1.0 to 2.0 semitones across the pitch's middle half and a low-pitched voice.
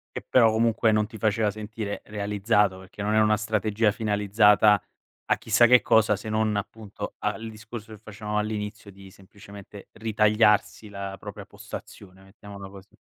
Yes: narrow, 1.4 semitones; low, 105 Hz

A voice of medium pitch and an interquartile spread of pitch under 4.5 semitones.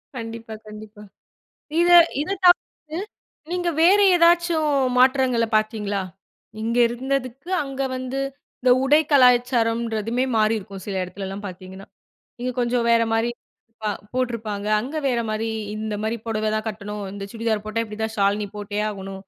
No: high, 225 Hz; average, 3.4 semitones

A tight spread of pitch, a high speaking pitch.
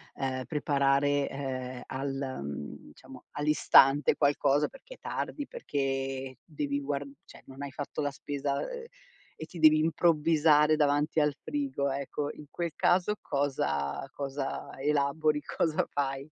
No: narrow, 1.9 semitones; medium, 145 Hz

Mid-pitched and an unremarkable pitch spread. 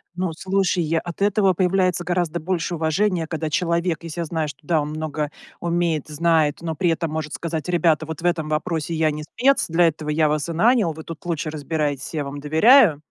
No: medium, 165 Hz; narrow, 2.3 semitones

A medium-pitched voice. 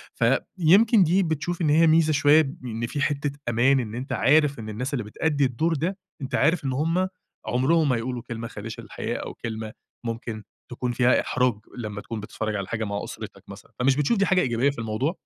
No: low, 130 Hz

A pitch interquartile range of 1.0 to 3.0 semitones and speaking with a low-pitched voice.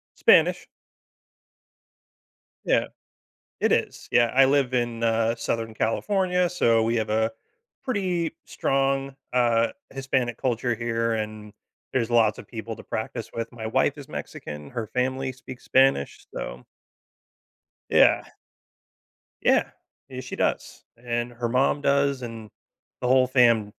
Yes: average, 2.7 semitones; low, 120 Hz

